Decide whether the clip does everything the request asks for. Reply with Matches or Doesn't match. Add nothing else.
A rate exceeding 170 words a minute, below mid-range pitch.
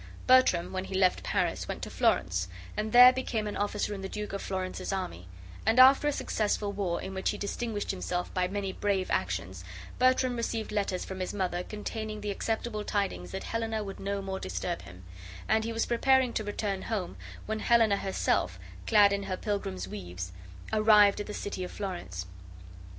Doesn't match